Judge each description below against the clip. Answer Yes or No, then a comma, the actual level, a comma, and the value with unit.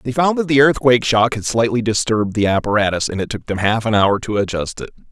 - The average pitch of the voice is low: Yes, low, 115 Hz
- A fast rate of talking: Yes, fast, 245 wpm